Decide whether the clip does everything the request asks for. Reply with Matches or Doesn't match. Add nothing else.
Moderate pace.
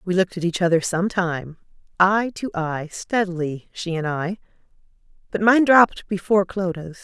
Matches